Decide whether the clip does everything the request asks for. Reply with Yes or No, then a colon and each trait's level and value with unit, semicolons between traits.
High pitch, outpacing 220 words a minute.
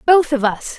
Yes: very high, 280 Hz; fast, 230 wpm